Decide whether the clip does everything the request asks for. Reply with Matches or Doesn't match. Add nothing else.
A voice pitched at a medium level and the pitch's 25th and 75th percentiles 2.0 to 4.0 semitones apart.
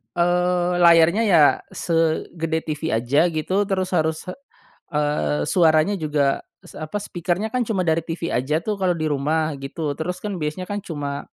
Matches